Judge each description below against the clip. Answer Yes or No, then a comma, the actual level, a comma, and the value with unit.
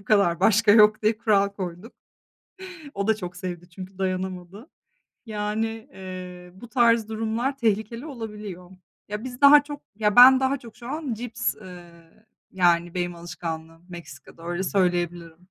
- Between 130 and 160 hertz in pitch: No, high, 200 Hz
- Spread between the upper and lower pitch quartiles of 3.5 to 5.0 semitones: Yes, average, 4.2 semitones